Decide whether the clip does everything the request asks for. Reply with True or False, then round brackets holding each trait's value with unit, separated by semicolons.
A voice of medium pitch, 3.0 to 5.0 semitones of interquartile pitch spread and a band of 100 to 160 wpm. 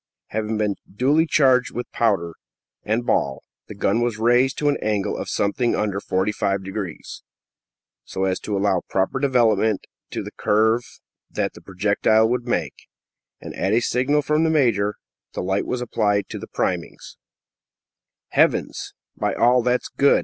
False (110 Hz; 3.7 semitones; 155 wpm)